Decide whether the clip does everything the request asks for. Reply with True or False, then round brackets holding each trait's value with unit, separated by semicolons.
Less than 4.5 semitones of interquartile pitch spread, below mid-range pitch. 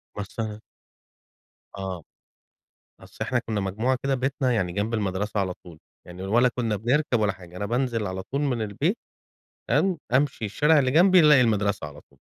False (4.9 semitones; 110 Hz)